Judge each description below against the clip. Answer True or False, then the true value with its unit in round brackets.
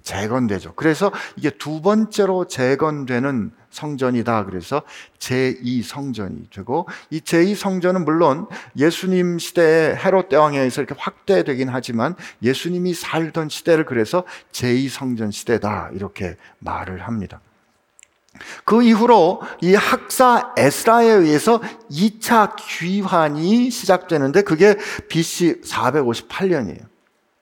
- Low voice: False (160 Hz)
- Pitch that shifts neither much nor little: False (7.1 semitones)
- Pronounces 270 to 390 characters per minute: False (250 characters per minute)